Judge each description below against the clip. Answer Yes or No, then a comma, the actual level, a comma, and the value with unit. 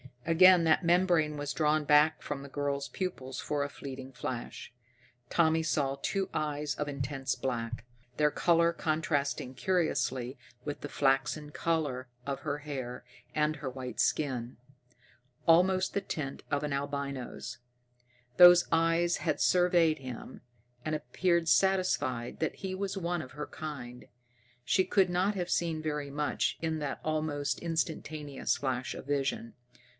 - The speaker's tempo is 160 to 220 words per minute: No, average, 140 wpm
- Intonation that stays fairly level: No, average, 3.4 semitones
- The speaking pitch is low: No, medium, 150 Hz